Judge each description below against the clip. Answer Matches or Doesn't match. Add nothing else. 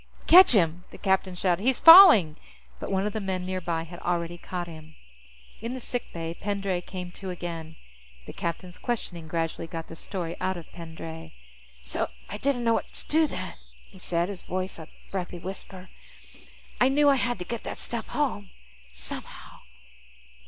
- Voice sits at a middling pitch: Matches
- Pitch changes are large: Doesn't match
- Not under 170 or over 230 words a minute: Matches